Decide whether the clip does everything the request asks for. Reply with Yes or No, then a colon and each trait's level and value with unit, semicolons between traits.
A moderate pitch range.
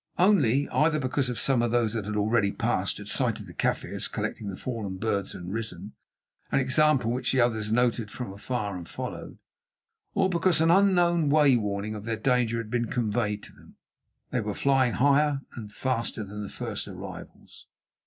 Yes: average, 4.4 semitones